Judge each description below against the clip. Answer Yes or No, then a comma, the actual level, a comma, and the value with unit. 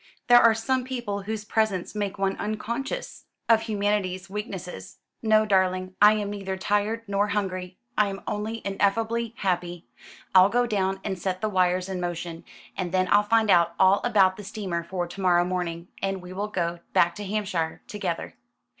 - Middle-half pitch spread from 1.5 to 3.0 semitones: Yes, narrow, 2.6 semitones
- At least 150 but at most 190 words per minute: Yes, average, 175 wpm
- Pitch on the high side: Yes, high, 195 Hz